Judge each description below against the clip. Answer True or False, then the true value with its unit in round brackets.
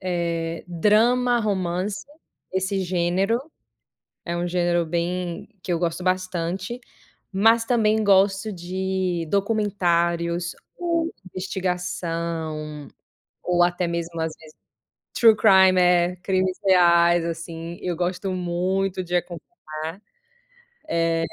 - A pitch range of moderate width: False (2.1 semitones)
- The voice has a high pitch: False (180 Hz)